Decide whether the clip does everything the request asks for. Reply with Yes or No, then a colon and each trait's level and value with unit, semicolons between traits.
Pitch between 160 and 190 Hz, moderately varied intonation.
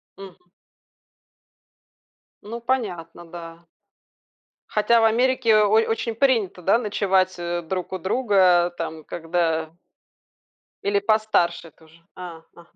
Yes: medium, 185 Hz; average, 4.4 semitones